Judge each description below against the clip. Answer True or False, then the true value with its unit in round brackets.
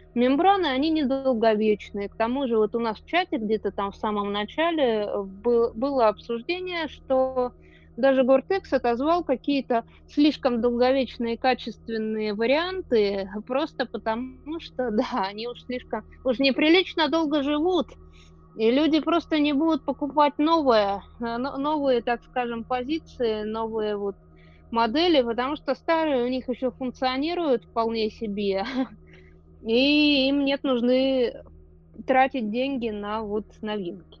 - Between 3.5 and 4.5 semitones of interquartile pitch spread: True (4.2 semitones)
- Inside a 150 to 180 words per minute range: False (125 wpm)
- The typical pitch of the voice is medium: False (250 Hz)